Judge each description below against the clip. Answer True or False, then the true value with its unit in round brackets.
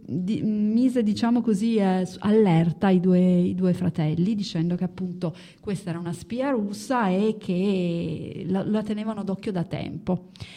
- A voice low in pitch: False (185 Hz)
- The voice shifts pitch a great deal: False (3.6 semitones)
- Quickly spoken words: False (155 wpm)